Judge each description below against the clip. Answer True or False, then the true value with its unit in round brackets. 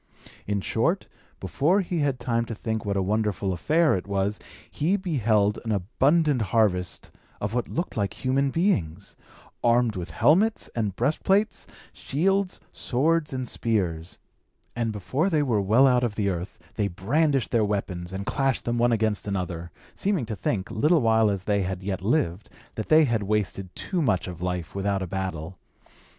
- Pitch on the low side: True (110 Hz)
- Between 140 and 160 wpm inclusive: False (170 wpm)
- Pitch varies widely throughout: True (6.1 semitones)